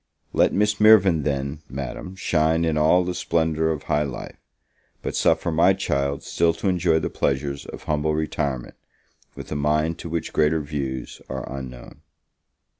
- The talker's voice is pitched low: Yes, very low, 80 Hz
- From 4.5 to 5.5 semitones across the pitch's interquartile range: No, average, 3.0 semitones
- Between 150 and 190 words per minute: Yes, average, 160 wpm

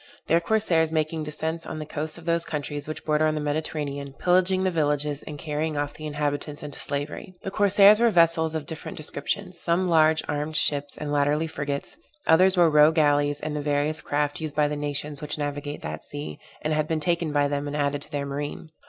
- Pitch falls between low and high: Yes, medium, 150 Hz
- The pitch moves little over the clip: Yes, narrow, 1.9 semitones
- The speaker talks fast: Yes, fast, 210 wpm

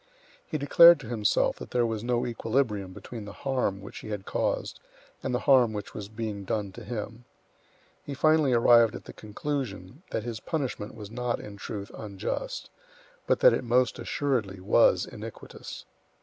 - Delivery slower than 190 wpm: Yes, average, 170 wpm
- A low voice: Yes, low, 115 Hz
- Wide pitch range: No, average, 3.7 semitones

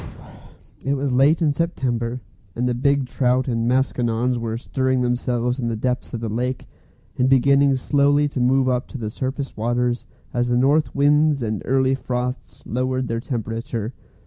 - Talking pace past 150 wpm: Yes, average, 170 wpm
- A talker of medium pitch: No, low, 125 Hz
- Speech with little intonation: Yes, narrow, 2.0 semitones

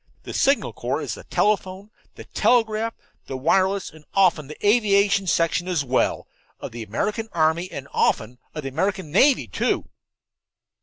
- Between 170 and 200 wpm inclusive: No, average, 155 wpm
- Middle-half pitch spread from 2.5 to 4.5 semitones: No, average, 5.3 semitones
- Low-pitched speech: No, medium, 185 Hz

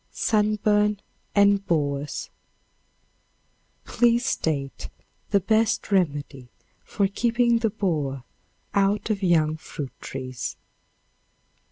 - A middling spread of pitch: No, wide, 6.3 semitones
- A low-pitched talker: No, high, 195 Hz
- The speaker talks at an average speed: No, slow, 85 wpm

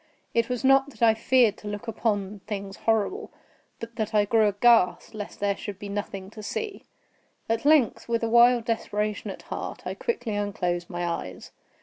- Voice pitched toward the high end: Yes, high, 215 Hz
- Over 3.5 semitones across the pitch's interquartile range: No, narrow, 2.6 semitones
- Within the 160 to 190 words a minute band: Yes, average, 185 wpm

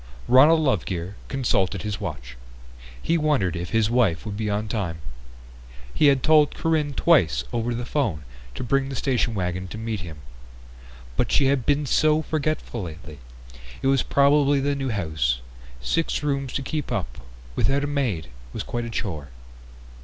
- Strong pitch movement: Yes, wide, 7.6 semitones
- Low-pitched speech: Yes, low, 120 Hz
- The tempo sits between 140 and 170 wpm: Yes, average, 165 wpm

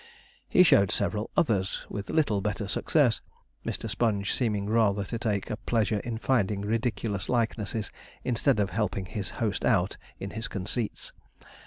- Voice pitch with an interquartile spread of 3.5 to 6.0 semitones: No, narrow, 2.6 semitones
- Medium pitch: No, low, 105 Hz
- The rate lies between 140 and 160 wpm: Yes, average, 150 wpm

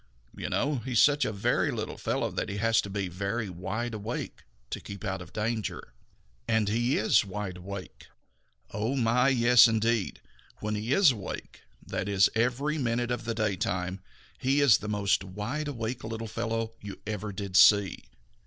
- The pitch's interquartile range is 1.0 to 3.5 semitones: Yes, average, 3.0 semitones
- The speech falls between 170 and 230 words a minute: Yes, average, 180 wpm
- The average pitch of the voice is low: Yes, low, 110 Hz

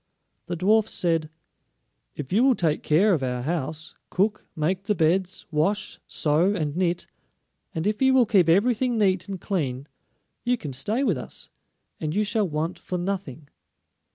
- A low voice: No, medium, 180 Hz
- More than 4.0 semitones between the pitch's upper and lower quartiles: Yes, average, 5.0 semitones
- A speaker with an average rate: Yes, average, 165 wpm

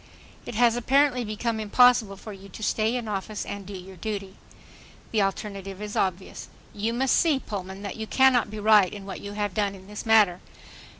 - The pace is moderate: Yes, average, 195 wpm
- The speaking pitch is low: No, high, 210 Hz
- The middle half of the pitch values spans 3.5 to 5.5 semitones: No, narrow, 2.6 semitones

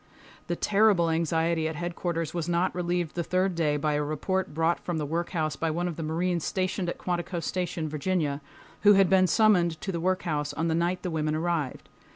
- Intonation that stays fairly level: Yes, narrow, 2.2 semitones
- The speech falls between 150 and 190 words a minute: No, average, 200 wpm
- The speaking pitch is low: No, medium, 170 Hz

